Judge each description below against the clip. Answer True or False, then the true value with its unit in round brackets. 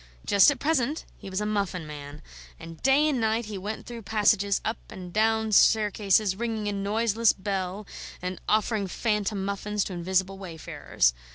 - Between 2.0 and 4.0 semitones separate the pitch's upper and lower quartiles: True (2.8 semitones)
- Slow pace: False (170 wpm)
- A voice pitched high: True (205 Hz)